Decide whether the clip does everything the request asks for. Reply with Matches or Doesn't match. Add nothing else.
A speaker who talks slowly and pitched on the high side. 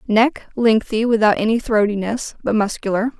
Matches